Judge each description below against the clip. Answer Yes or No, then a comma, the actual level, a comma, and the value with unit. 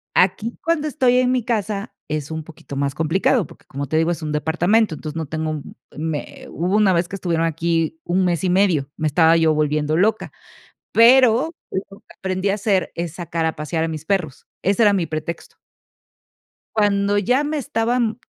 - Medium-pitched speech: Yes, medium, 175 Hz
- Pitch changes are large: No, average, 5.0 semitones